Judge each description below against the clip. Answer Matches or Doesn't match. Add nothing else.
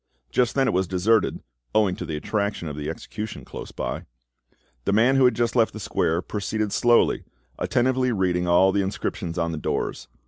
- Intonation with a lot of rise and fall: Doesn't match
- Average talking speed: Matches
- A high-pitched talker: Doesn't match